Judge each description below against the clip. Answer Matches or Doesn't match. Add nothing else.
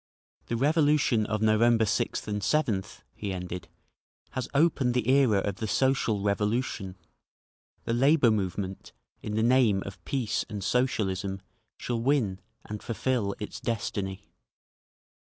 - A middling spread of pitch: Matches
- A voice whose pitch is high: Doesn't match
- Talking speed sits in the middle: Doesn't match